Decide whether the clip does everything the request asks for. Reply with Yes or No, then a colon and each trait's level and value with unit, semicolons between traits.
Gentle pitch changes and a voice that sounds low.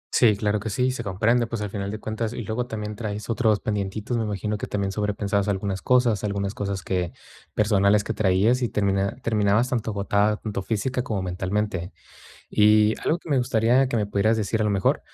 Yes: narrow, 2.2 semitones; low, 105 Hz